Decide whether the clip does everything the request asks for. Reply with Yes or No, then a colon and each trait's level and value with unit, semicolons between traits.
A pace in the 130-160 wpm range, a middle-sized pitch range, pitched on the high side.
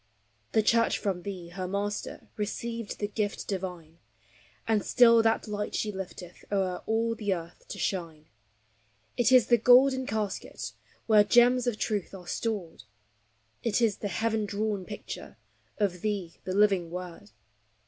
Yes: average, 150 wpm; average, 3.4 semitones; high, 205 Hz